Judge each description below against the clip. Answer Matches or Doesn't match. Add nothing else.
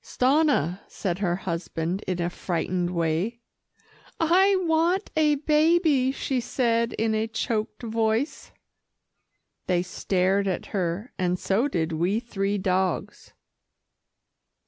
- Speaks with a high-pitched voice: Matches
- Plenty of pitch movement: Matches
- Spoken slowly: Matches